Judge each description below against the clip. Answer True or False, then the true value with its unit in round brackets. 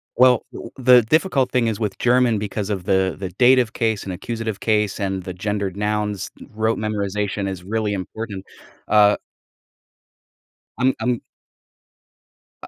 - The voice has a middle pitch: False (105 Hz)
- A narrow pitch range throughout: False (3.1 semitones)